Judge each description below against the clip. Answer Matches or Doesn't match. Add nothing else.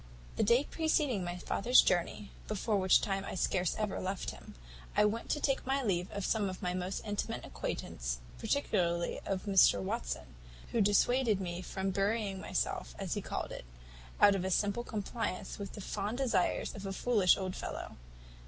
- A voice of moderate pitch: Doesn't match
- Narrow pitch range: Doesn't match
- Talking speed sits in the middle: Matches